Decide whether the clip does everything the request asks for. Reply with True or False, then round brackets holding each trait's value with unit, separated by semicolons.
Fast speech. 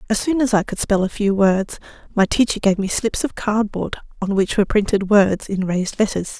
True (225 wpm)